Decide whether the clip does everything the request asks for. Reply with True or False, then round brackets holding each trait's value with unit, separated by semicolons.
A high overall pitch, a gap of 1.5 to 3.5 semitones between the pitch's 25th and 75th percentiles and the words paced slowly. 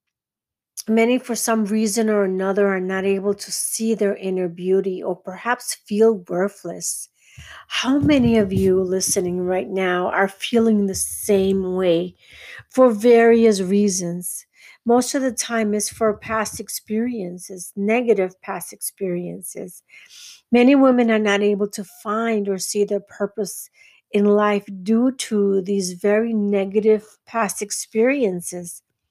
True (205 Hz; 2.9 semitones; 130 wpm)